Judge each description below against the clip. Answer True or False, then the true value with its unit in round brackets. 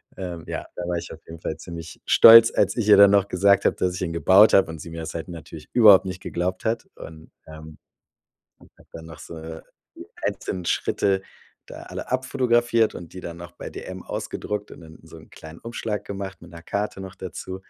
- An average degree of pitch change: True (3.6 semitones)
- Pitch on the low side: True (90 Hz)